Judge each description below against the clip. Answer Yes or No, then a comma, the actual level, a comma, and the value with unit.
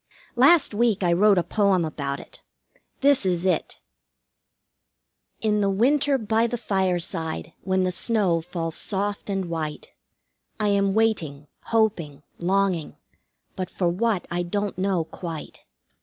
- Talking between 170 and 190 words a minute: No, slow, 135 wpm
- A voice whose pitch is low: No, high, 190 Hz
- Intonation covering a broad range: No, average, 3.8 semitones